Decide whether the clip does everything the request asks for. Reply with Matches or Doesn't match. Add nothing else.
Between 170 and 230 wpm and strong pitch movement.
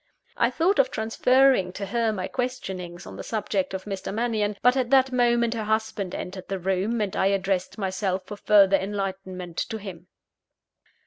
Doesn't match